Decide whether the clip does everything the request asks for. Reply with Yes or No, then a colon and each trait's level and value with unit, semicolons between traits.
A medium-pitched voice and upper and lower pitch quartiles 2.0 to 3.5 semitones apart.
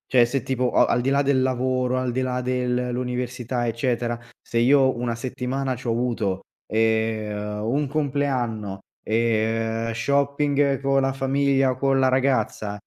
No: low, 125 Hz; narrow, 2.6 semitones